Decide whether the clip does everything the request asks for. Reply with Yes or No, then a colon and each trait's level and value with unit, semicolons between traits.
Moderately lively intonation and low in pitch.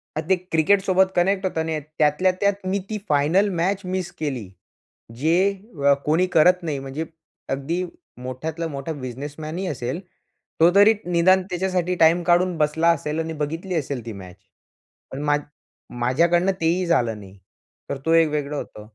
No: average, 3.9 semitones; medium, 160 Hz